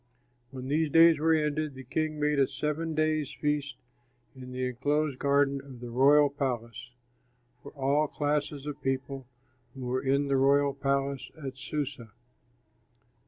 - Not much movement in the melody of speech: Yes, narrow, 2.0 semitones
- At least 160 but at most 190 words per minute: No, average, 150 wpm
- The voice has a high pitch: No, medium, 140 Hz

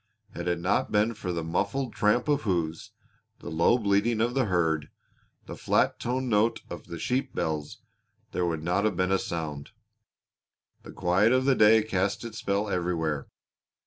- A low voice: Yes, low, 100 Hz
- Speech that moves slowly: No, average, 175 wpm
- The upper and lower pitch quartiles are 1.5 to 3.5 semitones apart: No, average, 5.0 semitones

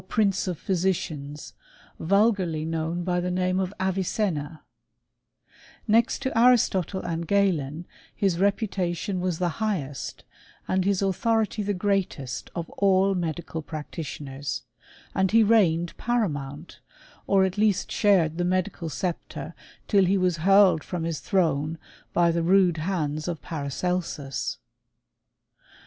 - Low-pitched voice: No, medium, 180 Hz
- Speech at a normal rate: No, slow, 125 wpm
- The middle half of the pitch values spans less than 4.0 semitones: Yes, average, 3.4 semitones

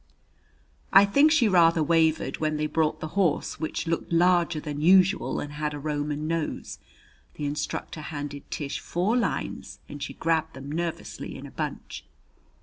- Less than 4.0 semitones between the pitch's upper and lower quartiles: Yes, narrow, 2.6 semitones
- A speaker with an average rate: Yes, average, 160 wpm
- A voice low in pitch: No, medium, 160 Hz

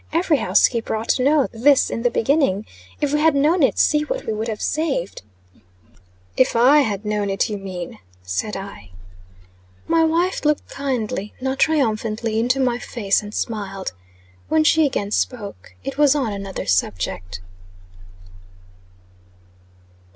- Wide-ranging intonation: Yes, wide, 6.0 semitones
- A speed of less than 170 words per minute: Yes, average, 145 wpm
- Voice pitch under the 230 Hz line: No, high, 235 Hz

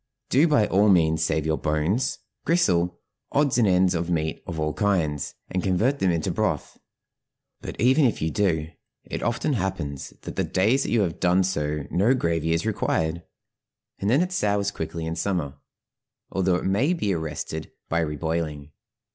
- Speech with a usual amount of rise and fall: Yes, average, 4.6 semitones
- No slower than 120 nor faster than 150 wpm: No, average, 170 wpm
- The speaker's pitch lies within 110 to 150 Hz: No, very low, 90 Hz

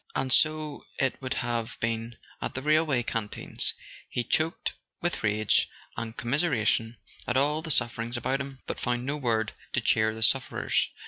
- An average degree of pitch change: Yes, average, 3.7 semitones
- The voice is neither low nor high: No, low, 120 Hz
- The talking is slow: No, average, 165 wpm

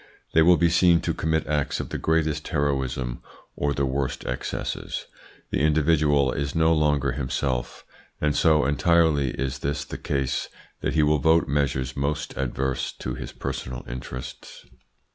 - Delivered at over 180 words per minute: No, average, 155 wpm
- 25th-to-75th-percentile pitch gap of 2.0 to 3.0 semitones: Yes, narrow, 2.5 semitones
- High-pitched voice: No, very low, 70 Hz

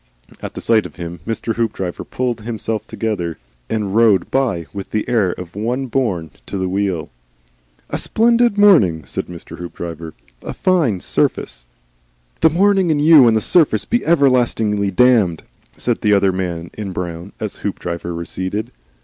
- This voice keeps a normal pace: Yes, average, 160 wpm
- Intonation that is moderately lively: No, wide, 6.2 semitones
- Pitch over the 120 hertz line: No, low, 105 Hz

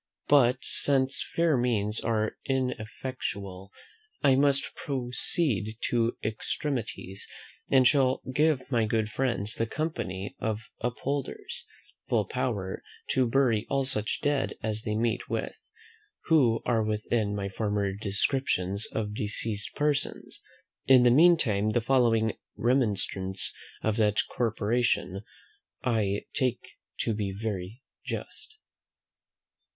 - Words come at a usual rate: No, slow, 115 wpm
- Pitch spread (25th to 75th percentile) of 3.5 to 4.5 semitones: Yes, average, 4.0 semitones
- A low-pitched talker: Yes, low, 115 Hz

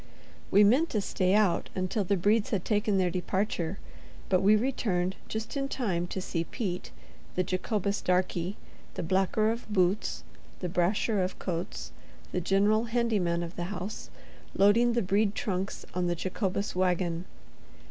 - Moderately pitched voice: No, high, 195 Hz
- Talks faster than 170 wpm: No, average, 155 wpm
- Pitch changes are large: No, average, 2.9 semitones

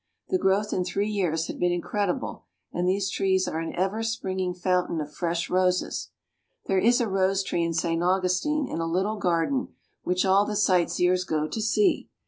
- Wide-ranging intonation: No, narrow, 2.4 semitones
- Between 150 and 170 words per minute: No, average, 190 wpm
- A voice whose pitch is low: No, medium, 185 Hz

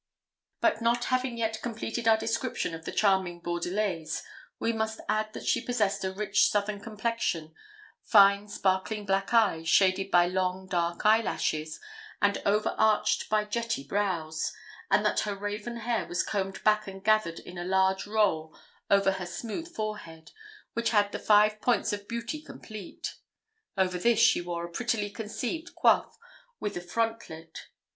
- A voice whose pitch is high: Yes, high, 205 Hz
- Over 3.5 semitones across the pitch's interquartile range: No, average, 3.0 semitones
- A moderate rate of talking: Yes, average, 160 wpm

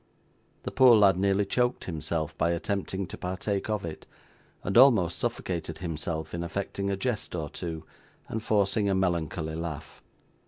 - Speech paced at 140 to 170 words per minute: Yes, average, 155 wpm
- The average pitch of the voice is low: Yes, very low, 95 Hz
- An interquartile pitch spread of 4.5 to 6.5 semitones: No, average, 3.4 semitones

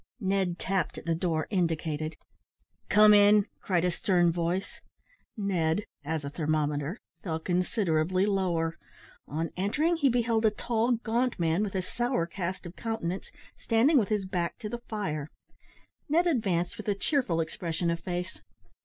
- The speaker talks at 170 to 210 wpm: No, average, 155 wpm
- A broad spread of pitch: No, average, 4.4 semitones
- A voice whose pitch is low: No, medium, 185 Hz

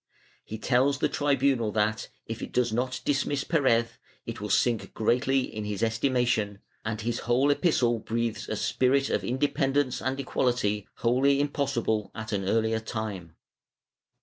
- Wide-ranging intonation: No, average, 3.6 semitones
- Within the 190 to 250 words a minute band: No, average, 150 wpm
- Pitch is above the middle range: No, low, 120 Hz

